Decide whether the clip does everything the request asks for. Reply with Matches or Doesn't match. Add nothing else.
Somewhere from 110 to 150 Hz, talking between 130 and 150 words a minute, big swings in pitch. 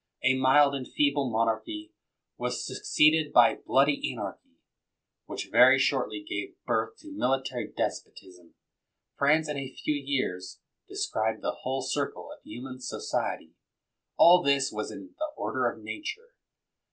Doesn't match